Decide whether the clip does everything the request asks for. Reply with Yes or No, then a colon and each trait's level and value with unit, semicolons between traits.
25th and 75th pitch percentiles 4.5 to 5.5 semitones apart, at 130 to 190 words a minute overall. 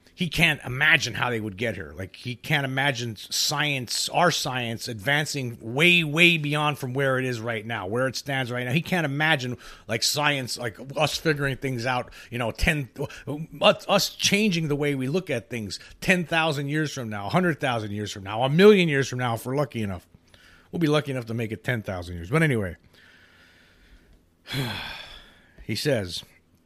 Yes: average, 5.2 semitones; average, 180 wpm